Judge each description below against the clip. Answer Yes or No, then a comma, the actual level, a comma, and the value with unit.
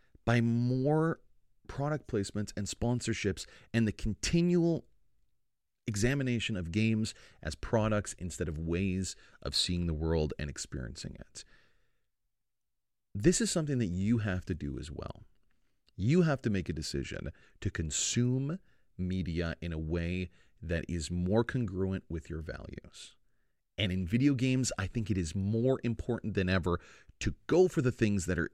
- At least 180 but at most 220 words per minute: No, average, 150 wpm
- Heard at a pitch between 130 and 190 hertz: No, low, 100 Hz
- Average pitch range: No, wide, 5.7 semitones